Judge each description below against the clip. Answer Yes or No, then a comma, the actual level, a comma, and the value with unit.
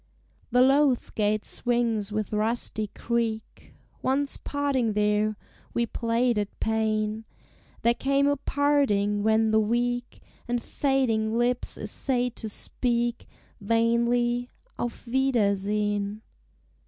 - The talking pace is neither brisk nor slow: No, slow, 105 wpm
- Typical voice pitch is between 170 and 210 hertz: No, high, 235 Hz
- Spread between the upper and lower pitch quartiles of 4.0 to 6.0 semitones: No, narrow, 2.5 semitones